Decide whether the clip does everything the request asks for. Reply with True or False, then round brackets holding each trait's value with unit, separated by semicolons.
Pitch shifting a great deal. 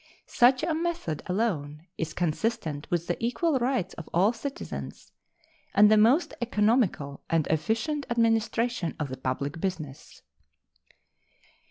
True (7.1 semitones)